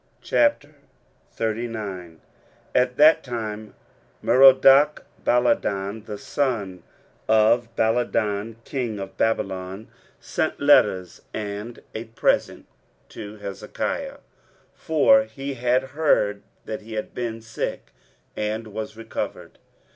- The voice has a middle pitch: No, low, 110 Hz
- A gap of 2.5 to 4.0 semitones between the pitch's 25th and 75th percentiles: Yes, average, 3.3 semitones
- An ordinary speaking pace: No, slow, 95 wpm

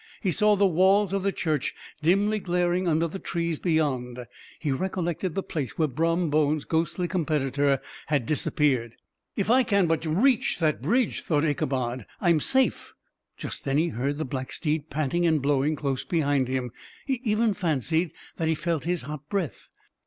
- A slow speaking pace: No, average, 175 wpm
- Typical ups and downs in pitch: Yes, average, 4.2 semitones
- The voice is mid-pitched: Yes, medium, 160 Hz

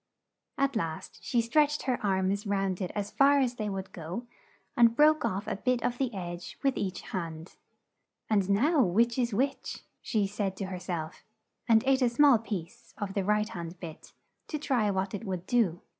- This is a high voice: Yes, high, 210 Hz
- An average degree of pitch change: Yes, average, 4.6 semitones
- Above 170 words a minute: Yes, average, 190 wpm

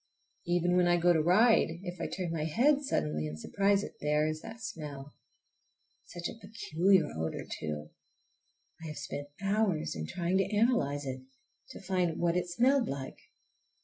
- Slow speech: No, average, 165 wpm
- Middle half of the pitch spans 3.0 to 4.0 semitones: No, average, 4.9 semitones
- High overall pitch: No, medium, 175 Hz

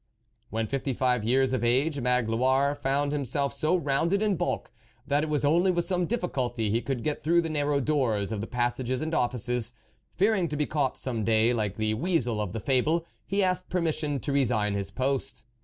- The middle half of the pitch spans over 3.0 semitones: Yes, average, 4.6 semitones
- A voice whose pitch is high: No, low, 135 Hz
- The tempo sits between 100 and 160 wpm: No, average, 195 wpm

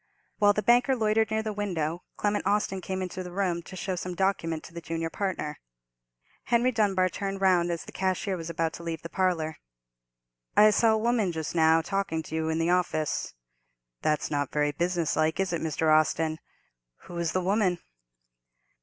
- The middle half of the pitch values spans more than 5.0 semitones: No, average, 3.5 semitones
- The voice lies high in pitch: No, medium, 180 Hz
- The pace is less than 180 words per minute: No, average, 190 wpm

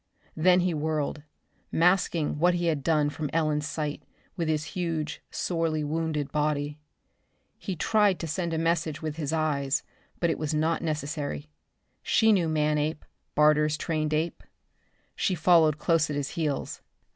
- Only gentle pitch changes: Yes, narrow, 1.7 semitones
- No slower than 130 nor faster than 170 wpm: Yes, average, 155 wpm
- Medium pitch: Yes, medium, 155 Hz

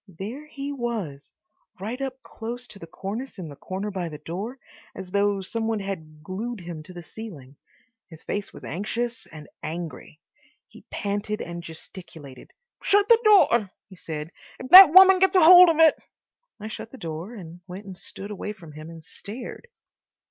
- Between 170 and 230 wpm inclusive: Yes, average, 175 wpm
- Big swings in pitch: Yes, wide, 6.4 semitones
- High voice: Yes, high, 200 Hz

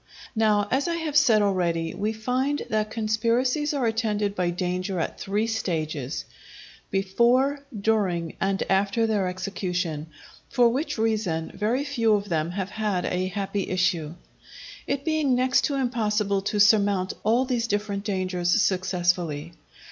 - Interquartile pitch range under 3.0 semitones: No, average, 4.0 semitones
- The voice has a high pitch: Yes, high, 205 Hz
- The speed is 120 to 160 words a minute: Yes, average, 140 wpm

